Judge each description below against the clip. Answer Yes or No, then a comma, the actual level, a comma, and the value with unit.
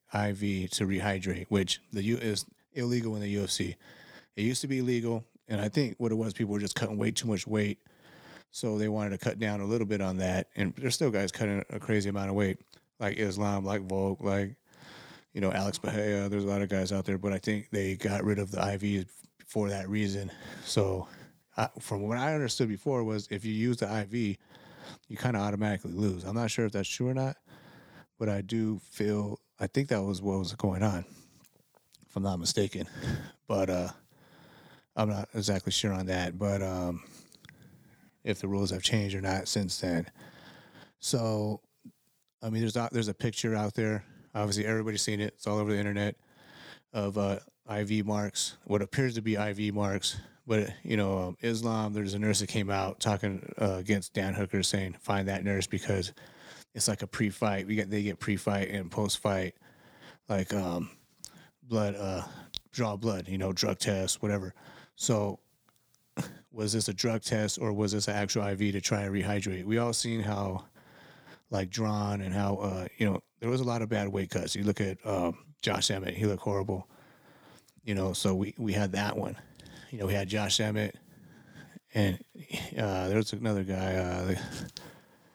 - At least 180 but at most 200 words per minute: Yes, average, 195 wpm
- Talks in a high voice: No, low, 105 Hz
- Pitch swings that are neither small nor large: No, narrow, 2.0 semitones